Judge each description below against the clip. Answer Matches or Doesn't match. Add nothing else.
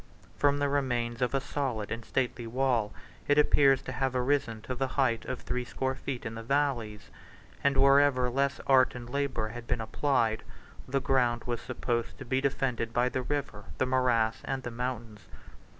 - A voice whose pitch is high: Doesn't match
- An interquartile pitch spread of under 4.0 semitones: Matches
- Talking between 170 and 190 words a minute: Matches